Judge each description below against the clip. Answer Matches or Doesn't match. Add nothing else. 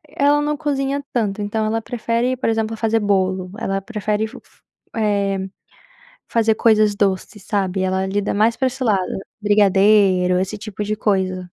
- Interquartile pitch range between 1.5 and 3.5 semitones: Matches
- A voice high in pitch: Matches